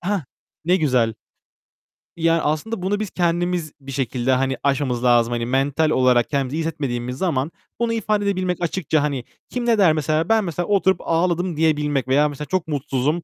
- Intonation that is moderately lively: Yes, average, 5.0 semitones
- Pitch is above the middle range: No, medium, 155 Hz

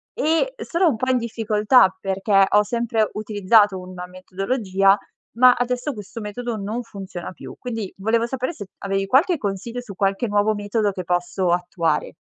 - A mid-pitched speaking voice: No, high, 210 Hz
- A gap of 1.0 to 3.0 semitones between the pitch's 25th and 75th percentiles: No, average, 3.7 semitones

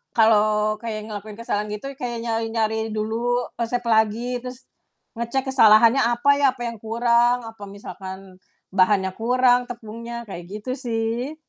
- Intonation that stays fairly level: Yes, narrow, 2.3 semitones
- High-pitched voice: Yes, high, 225 Hz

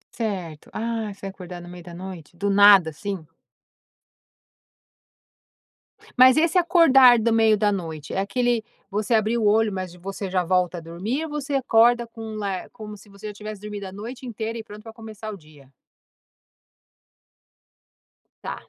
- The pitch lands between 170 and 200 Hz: No, high, 210 Hz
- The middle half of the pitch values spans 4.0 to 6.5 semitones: No, average, 3.4 semitones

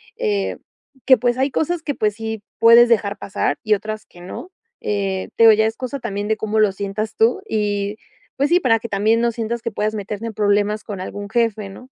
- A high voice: Yes, high, 215 Hz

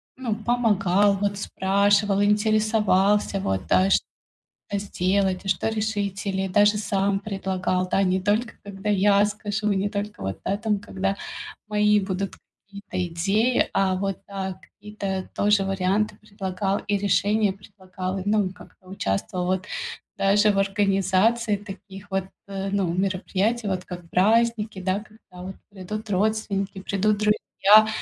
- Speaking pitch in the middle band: No, high, 200 Hz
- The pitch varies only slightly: Yes, narrow, 1.6 semitones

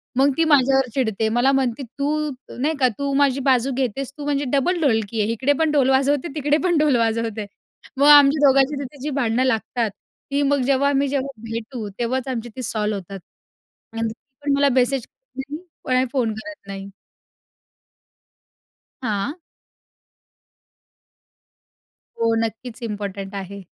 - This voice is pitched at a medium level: No, very high, 260 Hz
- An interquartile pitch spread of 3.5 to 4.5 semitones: Yes, average, 3.9 semitones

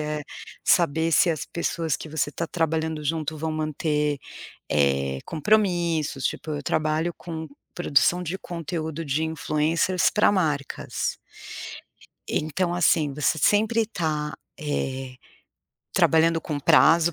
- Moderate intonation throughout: No, narrow, 2.1 semitones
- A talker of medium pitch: Yes, medium, 160 Hz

